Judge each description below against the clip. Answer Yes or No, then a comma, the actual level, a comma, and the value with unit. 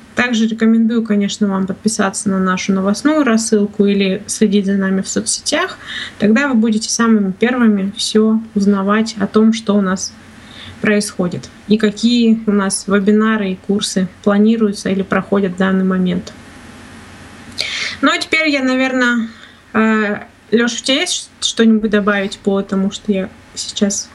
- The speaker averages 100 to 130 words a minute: No, average, 140 wpm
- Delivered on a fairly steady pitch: Yes, narrow, 2.3 semitones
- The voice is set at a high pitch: Yes, high, 210 Hz